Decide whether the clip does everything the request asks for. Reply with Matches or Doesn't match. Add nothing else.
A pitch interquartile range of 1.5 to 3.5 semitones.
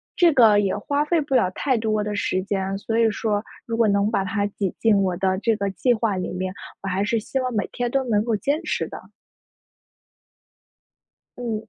Matches